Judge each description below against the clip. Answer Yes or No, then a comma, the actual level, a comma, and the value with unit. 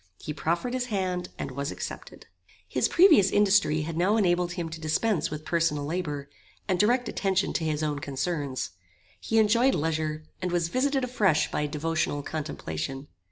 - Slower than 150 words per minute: No, average, 160 wpm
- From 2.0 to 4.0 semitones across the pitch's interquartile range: No, average, 5.1 semitones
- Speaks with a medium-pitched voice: Yes, medium, 170 Hz